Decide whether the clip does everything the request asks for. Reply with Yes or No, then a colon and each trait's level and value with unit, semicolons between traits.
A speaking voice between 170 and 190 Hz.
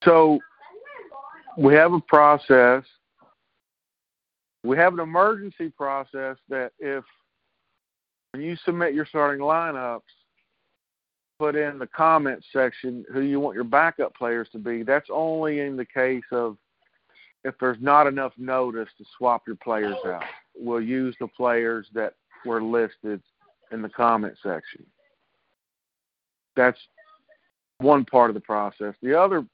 No: low, 130 Hz